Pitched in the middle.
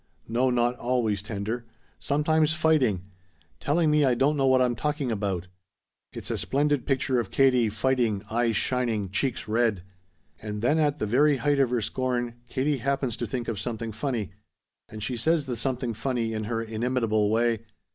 No: low, 120 Hz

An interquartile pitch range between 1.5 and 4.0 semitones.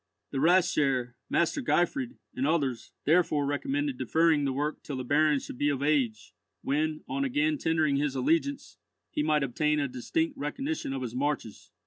No: average, 4.4 semitones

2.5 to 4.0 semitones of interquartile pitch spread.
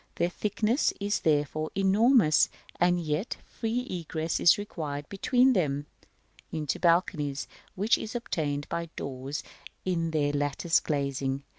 No: wide, 5.6 semitones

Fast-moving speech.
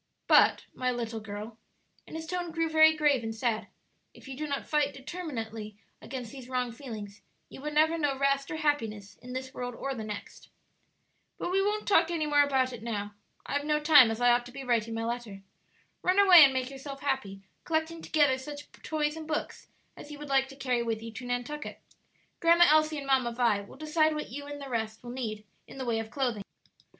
Yes: fast, 215 wpm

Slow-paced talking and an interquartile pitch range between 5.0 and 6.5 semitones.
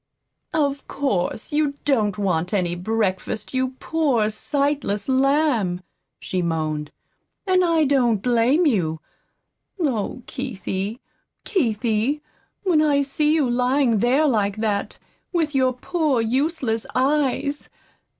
Yes: slow, 110 wpm; wide, 5.6 semitones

